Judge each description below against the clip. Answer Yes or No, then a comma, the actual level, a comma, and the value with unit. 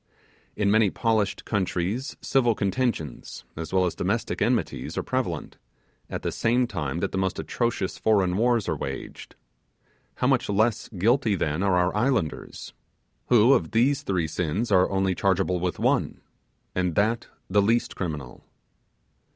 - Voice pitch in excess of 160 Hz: No, low, 100 Hz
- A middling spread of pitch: Yes, average, 4.2 semitones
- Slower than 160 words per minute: Yes, average, 150 wpm